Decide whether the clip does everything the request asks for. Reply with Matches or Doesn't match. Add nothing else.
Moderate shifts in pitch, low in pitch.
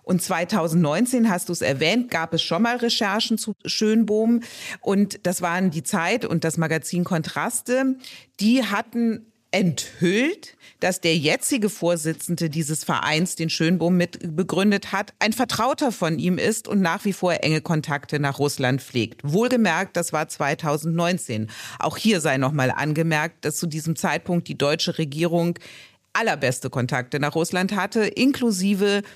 Doesn't match